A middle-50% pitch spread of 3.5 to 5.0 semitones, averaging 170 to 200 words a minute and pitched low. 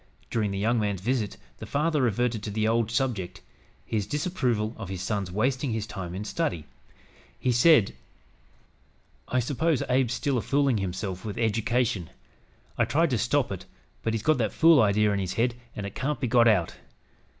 Yes: average, 4.0 semitones; average, 185 wpm; low, 115 Hz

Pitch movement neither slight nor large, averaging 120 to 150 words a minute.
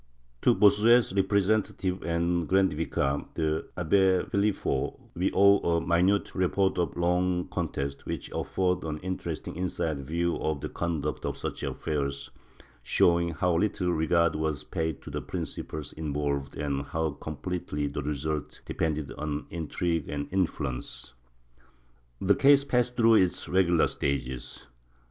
Yes: average, 3.9 semitones; average, 140 wpm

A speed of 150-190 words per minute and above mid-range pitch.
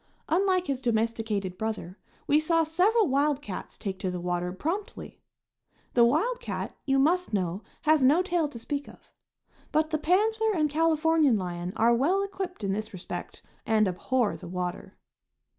Yes: average, 160 wpm; very high, 275 Hz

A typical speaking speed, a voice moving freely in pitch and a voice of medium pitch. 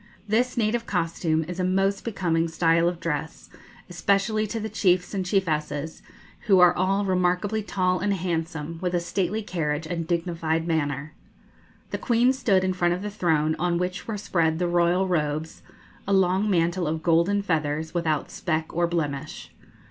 No: average, 165 wpm; average, 3.0 semitones; medium, 175 Hz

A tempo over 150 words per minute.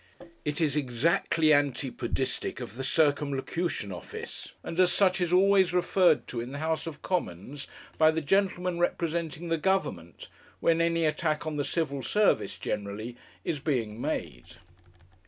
No: average, 145 wpm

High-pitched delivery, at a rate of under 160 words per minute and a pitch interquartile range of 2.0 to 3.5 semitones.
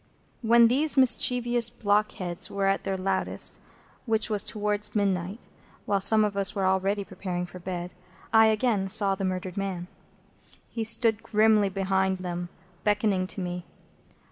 Yes: high, 200 Hz; average, 145 wpm; average, 2.7 semitones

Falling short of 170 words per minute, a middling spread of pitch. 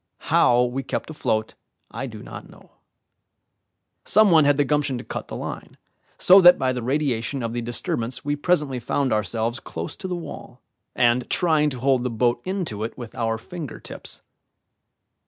No: average, 180 wpm; average, 4.1 semitones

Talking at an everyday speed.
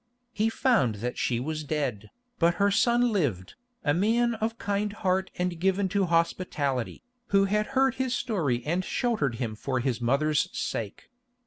Yes: average, 160 wpm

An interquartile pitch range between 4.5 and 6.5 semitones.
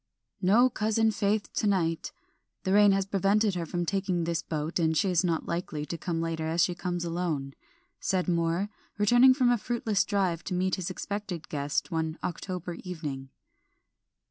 No: average, 3.4 semitones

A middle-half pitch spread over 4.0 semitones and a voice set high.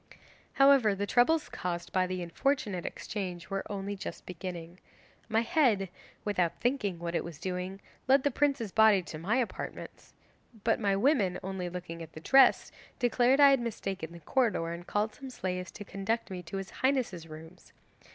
Yes: average, 5.2 semitones; high, 195 Hz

